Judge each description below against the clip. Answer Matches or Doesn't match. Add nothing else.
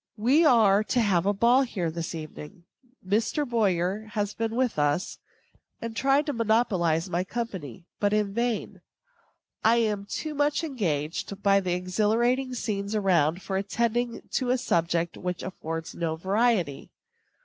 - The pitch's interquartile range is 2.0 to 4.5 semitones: Doesn't match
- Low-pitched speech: Doesn't match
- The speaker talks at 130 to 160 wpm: Matches